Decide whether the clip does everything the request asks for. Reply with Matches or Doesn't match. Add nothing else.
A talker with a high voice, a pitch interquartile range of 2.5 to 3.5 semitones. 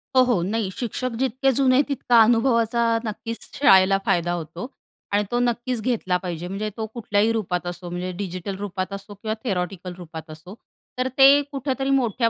Doesn't match